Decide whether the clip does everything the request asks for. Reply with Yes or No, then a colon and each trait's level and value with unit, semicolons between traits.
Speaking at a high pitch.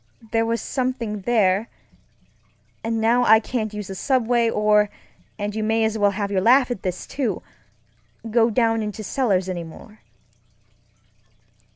Yes: high, 220 Hz